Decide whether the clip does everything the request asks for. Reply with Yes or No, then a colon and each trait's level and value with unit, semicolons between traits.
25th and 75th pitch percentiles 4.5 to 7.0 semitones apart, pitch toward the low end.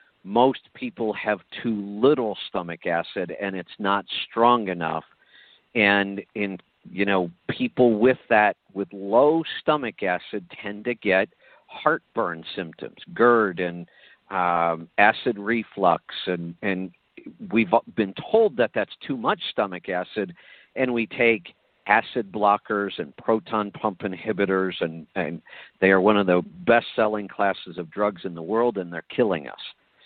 No: average, 3.5 semitones; low, 105 Hz